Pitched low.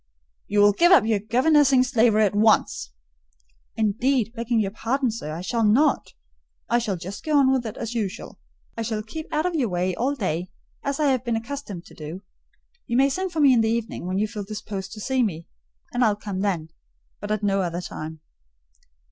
No: high, 220 Hz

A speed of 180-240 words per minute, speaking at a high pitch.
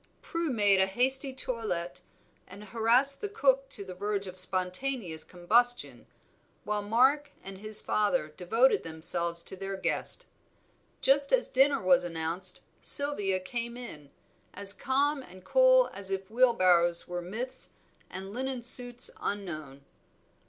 No: slow, 135 wpm; high, 205 Hz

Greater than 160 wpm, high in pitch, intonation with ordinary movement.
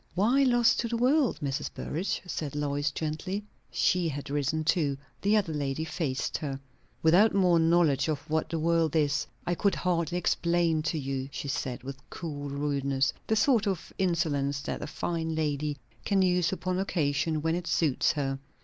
No: average, 175 wpm; medium, 160 Hz; average, 4.0 semitones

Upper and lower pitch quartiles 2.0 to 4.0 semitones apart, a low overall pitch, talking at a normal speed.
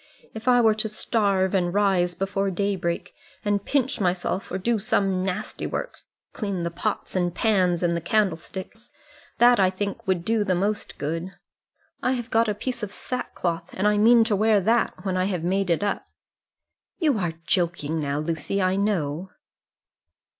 No: average, 3.4 semitones; high, 195 Hz; average, 175 wpm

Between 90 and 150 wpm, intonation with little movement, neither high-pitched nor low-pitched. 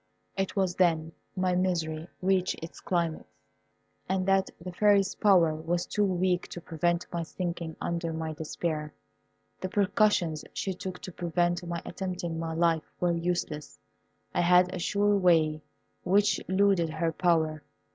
Yes: average, 145 wpm; narrow, 2.2 semitones; medium, 175 Hz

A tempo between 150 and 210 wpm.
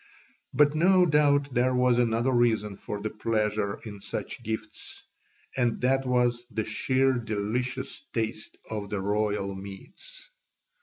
No: slow, 135 wpm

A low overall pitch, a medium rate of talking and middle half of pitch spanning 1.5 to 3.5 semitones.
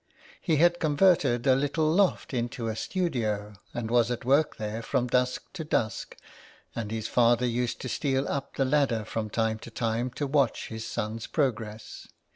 No: low, 120 Hz; average, 175 wpm; average, 4.1 semitones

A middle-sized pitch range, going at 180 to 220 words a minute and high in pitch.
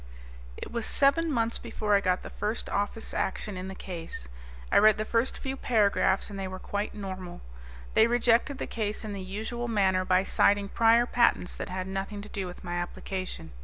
Yes: average, 3.4 semitones; average, 200 wpm; high, 205 Hz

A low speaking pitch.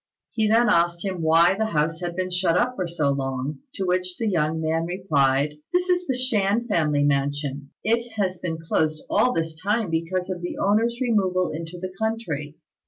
No: medium, 180 Hz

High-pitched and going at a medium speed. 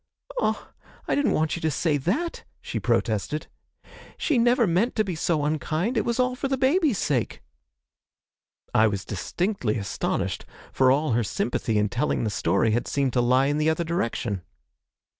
No: medium, 155 Hz; average, 175 wpm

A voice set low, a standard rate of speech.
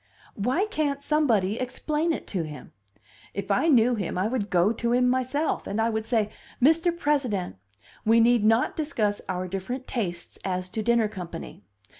No: high, 230 Hz; average, 170 wpm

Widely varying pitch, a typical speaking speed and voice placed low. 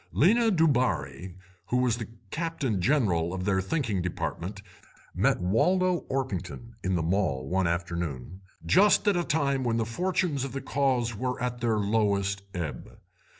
Yes: wide, 7.0 semitones; average, 150 wpm; low, 115 Hz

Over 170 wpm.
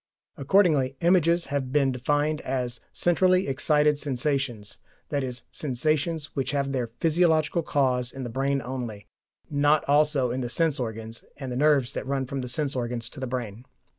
No: average, 165 wpm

